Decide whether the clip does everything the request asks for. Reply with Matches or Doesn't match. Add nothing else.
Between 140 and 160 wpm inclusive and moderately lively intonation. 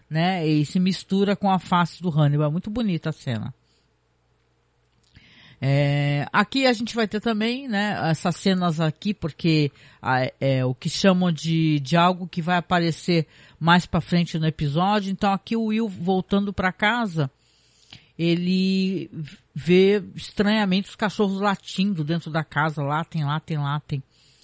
Matches